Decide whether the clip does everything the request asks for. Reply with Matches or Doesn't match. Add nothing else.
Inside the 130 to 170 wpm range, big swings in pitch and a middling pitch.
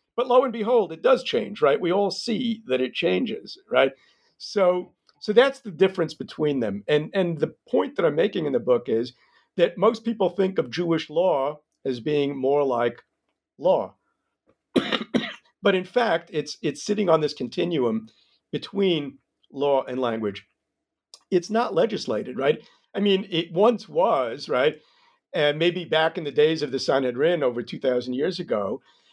Matches